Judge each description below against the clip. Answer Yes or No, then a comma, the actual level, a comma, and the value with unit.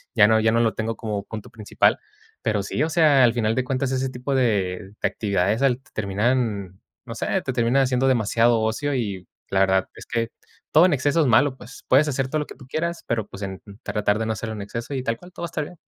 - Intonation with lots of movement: No, average, 3.9 semitones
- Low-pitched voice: Yes, low, 115 Hz